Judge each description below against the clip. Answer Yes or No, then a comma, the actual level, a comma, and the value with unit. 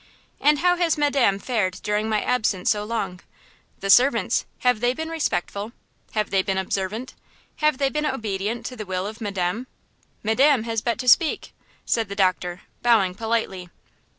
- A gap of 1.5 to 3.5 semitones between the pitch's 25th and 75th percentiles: No, average, 4.7 semitones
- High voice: Yes, high, 220 Hz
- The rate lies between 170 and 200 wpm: No, average, 160 wpm